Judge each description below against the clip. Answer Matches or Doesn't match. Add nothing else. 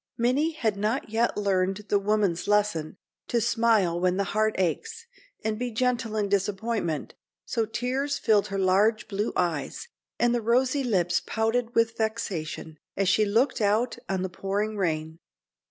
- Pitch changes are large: Doesn't match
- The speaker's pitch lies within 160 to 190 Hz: Doesn't match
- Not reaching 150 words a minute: Doesn't match